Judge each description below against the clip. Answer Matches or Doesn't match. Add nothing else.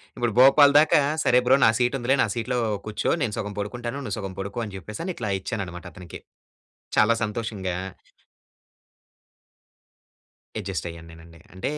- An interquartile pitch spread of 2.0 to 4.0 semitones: Doesn't match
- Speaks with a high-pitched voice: Doesn't match